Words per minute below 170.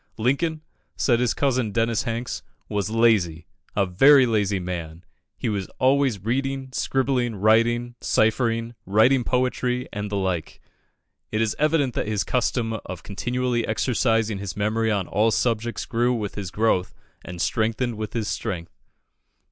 Yes: average, 145 wpm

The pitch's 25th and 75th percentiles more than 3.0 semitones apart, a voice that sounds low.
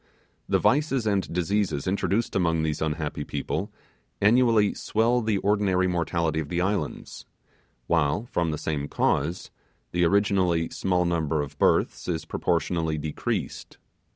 Yes: average, 4.3 semitones; very low, 85 Hz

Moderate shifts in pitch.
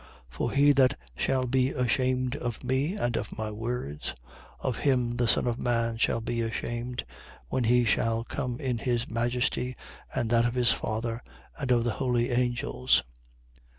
No: narrow, 1.6 semitones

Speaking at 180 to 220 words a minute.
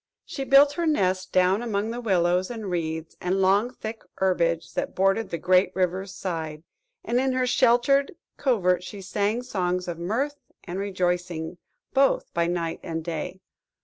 No: average, 160 wpm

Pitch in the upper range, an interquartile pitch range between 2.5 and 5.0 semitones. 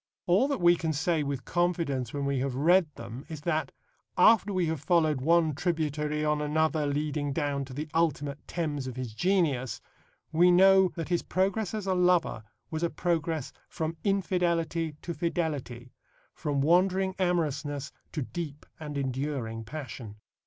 No: medium, 155 Hz; average, 3.7 semitones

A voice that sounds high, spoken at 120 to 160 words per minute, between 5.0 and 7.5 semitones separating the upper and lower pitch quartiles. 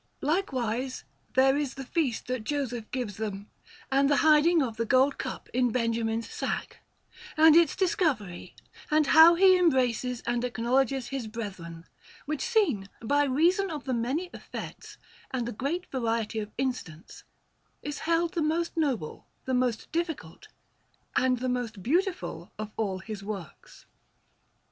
Yes: very high, 255 Hz; average, 145 wpm; average, 5.3 semitones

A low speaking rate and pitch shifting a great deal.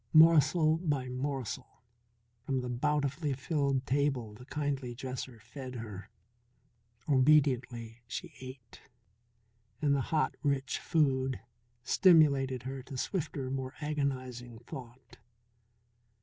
No: slow, 105 wpm; narrow, 2.5 semitones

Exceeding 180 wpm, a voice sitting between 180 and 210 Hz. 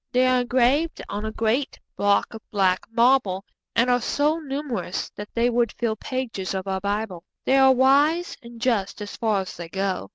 No: average, 190 wpm; high, 230 Hz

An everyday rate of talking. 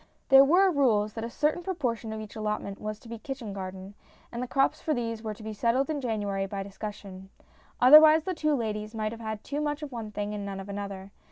No: fast, 235 wpm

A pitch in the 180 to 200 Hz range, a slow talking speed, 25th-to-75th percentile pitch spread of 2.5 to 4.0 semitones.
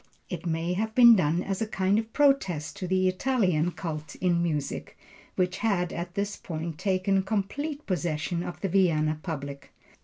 No: medium, 185 Hz; average, 165 wpm; average, 3.4 semitones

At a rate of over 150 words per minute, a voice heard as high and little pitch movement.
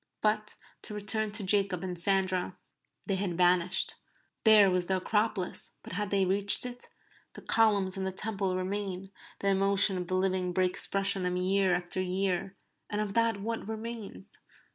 Yes: average, 170 wpm; high, 195 Hz; narrow, 2.1 semitones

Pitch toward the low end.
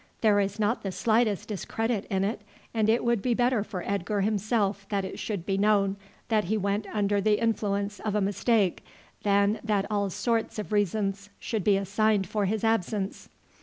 No: high, 205 Hz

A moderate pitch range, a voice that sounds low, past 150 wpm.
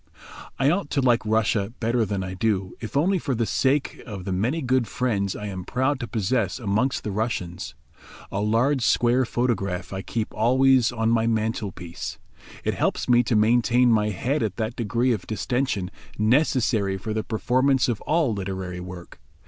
Yes: average, 4.2 semitones; low, 115 Hz; average, 180 wpm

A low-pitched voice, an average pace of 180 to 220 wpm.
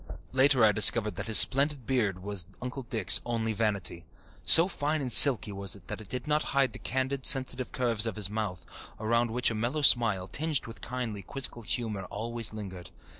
Yes: low, 115 Hz; average, 190 wpm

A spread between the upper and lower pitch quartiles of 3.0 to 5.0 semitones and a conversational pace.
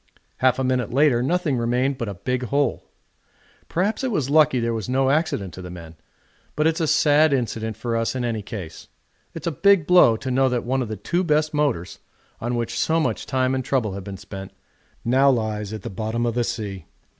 No: average, 4.6 semitones; fast, 215 wpm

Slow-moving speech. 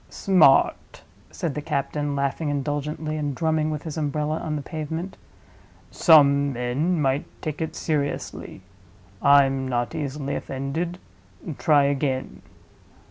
Yes: slow, 120 wpm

